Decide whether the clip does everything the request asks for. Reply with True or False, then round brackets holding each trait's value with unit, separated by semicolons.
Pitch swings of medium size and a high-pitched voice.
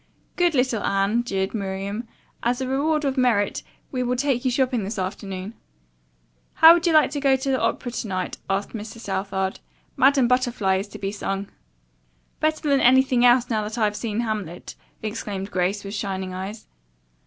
True (4.7 semitones; 225 Hz)